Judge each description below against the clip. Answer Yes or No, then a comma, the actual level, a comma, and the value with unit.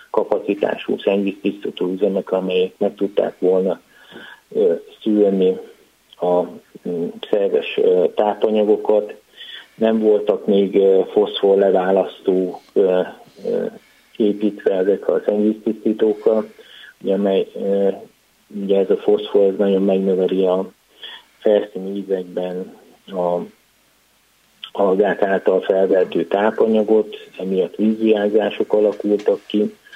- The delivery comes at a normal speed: No, slow, 75 wpm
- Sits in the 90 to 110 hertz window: Yes, low, 105 Hz